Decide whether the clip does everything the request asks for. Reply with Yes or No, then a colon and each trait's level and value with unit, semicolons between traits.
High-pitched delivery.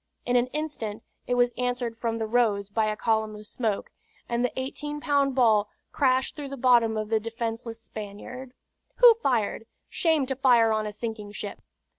Yes: high, 235 Hz